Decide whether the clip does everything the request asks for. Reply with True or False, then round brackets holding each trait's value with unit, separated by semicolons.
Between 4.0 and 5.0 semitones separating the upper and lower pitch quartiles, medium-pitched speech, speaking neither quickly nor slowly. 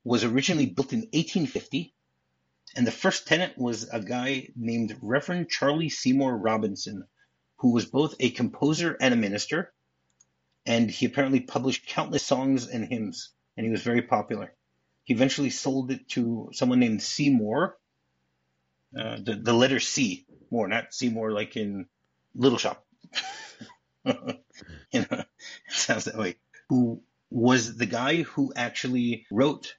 False (4.4 semitones; 120 Hz; 145 wpm)